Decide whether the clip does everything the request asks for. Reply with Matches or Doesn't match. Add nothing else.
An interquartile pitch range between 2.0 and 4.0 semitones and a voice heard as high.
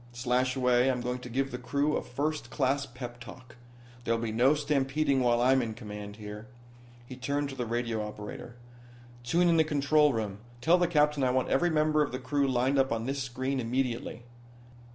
Doesn't match